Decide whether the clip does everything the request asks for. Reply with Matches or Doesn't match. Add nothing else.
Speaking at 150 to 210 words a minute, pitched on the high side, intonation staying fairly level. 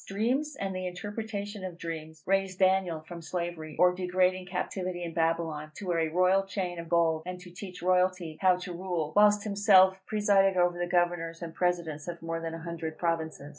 Doesn't match